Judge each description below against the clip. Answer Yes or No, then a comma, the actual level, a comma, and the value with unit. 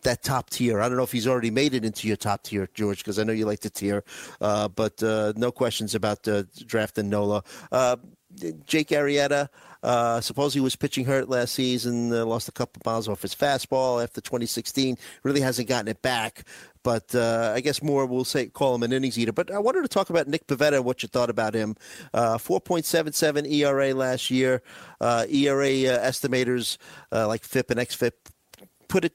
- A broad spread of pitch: No, average, 3.7 semitones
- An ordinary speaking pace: No, fast, 210 wpm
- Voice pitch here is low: Yes, low, 125 Hz